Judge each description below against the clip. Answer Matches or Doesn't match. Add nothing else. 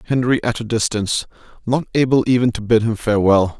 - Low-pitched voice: Matches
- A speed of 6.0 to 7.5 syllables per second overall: Matches